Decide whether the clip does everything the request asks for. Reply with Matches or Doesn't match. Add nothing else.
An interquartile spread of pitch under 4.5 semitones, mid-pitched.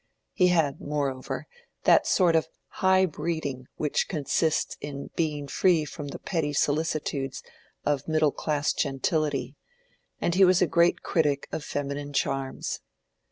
Matches